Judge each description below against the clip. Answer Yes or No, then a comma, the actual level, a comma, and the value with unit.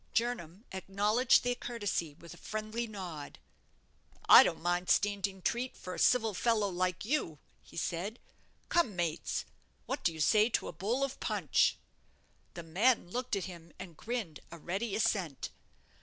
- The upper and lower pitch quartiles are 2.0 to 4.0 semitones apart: No, average, 5.0 semitones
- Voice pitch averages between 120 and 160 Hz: No, high, 200 Hz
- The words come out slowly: No, average, 155 wpm